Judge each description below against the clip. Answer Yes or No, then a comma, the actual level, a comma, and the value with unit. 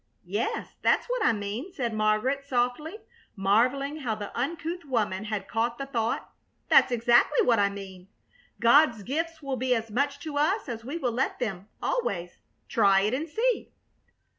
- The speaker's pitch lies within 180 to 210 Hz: No, high, 245 Hz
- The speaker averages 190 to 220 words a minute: No, average, 165 wpm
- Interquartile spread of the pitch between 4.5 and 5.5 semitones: Yes, average, 5.2 semitones